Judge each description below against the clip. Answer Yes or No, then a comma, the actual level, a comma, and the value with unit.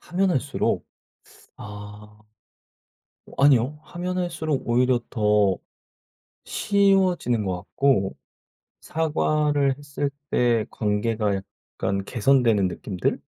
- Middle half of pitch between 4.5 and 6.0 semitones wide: No, wide, 6.4 semitones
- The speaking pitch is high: No, low, 125 Hz